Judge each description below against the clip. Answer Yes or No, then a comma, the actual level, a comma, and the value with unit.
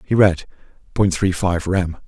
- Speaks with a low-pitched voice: Yes, very low, 90 Hz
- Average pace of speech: Yes, average, 175 wpm